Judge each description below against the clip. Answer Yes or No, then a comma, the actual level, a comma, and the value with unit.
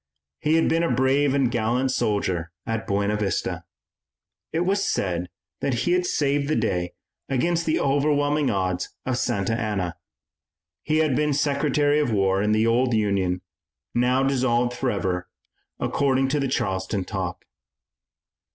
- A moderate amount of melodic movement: No, wide, 6.1 semitones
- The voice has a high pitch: No, low, 125 Hz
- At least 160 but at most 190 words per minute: No, average, 145 wpm